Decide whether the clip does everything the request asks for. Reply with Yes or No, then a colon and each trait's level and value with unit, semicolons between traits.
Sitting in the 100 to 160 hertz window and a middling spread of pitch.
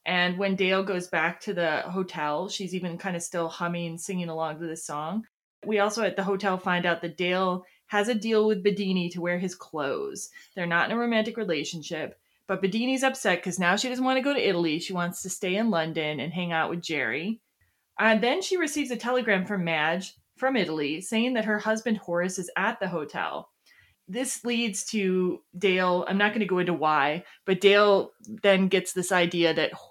No: high, 190 Hz; average, 3.8 semitones